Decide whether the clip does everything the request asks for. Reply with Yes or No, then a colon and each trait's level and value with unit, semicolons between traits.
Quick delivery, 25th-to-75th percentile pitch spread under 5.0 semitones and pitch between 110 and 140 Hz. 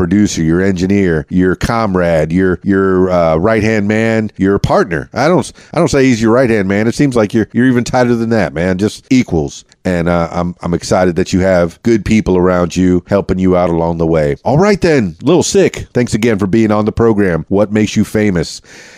No: fast, 220 wpm; average, 3.8 semitones; low, 100 Hz